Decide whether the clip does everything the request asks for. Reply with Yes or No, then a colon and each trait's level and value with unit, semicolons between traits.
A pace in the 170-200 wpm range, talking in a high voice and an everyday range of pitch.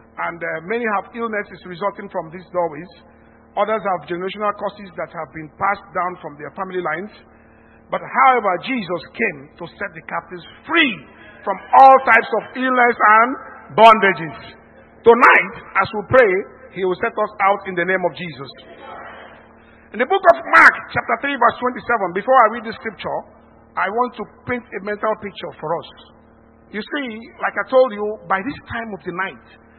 Yes: average, 175 wpm; high, 200 Hz; average, 4.6 semitones